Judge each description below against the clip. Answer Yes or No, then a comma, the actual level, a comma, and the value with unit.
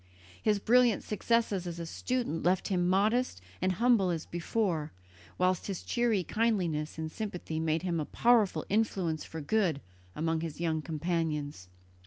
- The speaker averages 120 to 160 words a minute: Yes, average, 150 wpm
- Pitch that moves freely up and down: No, average, 5.0 semitones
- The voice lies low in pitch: No, medium, 180 Hz